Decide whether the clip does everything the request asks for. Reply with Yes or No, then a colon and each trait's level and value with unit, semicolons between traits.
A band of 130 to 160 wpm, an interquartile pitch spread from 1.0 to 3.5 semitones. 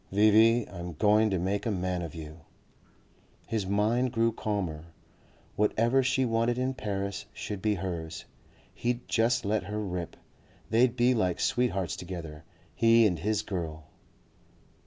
No: average, 140 wpm; average, 4.1 semitones